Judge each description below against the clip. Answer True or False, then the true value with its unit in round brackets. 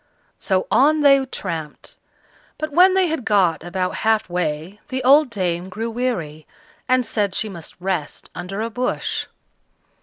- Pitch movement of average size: False (6.4 semitones)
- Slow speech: False (150 wpm)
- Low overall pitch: False (210 Hz)